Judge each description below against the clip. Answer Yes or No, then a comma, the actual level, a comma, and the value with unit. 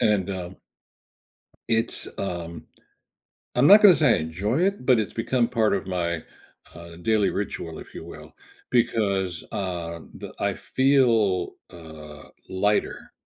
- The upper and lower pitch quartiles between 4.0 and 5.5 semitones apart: Yes, average, 5.2 semitones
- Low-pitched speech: Yes, low, 100 Hz